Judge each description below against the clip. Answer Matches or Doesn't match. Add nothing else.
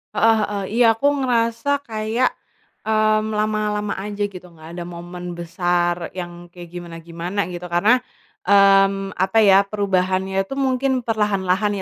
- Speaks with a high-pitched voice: Matches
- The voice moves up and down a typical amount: Matches